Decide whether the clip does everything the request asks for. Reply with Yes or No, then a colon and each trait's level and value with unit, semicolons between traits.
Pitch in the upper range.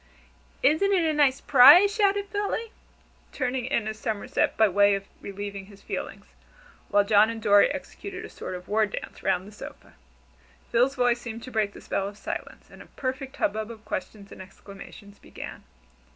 Yes: high, 220 Hz